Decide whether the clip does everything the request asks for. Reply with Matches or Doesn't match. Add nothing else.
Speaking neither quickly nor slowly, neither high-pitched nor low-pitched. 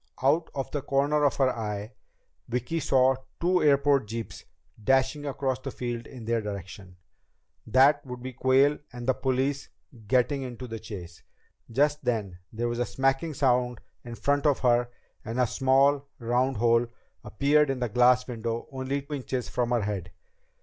Doesn't match